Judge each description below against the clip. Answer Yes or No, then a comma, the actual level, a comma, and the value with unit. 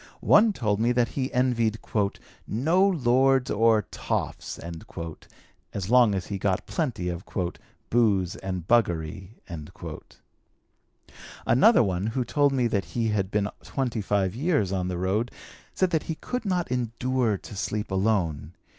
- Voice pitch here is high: No, low, 110 Hz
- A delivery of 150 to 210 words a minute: No, average, 140 wpm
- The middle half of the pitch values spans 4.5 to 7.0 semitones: Yes, average, 5.0 semitones